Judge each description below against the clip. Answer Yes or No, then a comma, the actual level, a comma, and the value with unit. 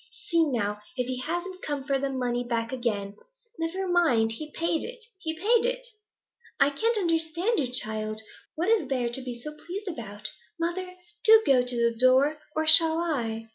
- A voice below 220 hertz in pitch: No, very high, 290 Hz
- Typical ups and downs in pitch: No, wide, 6.3 semitones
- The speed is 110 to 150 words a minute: No, average, 180 wpm